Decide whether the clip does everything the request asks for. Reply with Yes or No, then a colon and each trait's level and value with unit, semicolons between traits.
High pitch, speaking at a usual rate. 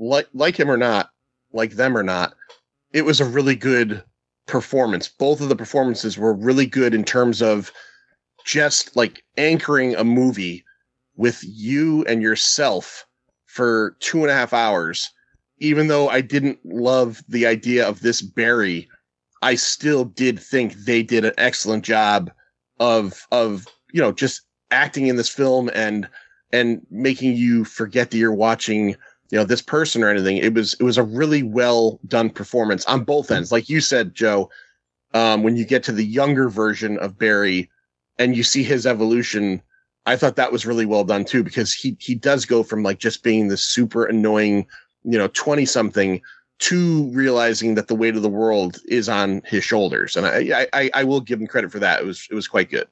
No: low, 115 Hz; average, 185 wpm